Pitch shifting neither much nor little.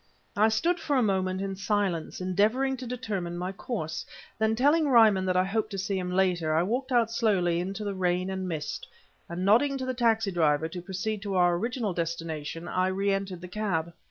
Yes: average, 3.8 semitones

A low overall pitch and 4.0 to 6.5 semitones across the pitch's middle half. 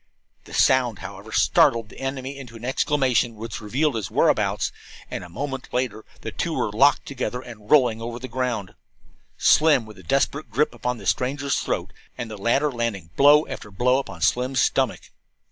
No: low, 125 Hz; average, 3.5 semitones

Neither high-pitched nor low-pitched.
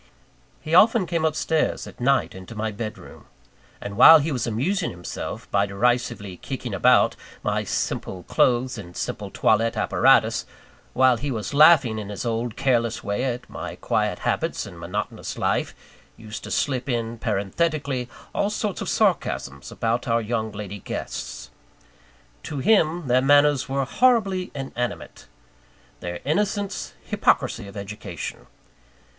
No: low, 120 Hz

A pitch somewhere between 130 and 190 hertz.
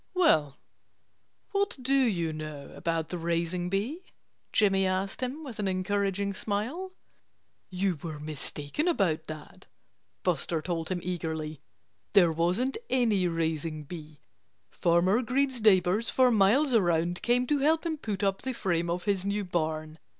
Yes: medium, 185 Hz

